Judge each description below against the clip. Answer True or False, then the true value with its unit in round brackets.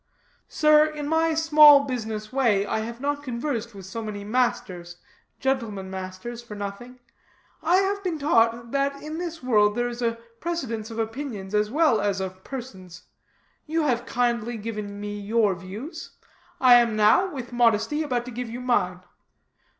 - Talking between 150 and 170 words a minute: True (165 wpm)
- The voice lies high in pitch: True (235 Hz)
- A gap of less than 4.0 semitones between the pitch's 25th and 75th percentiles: False (5.1 semitones)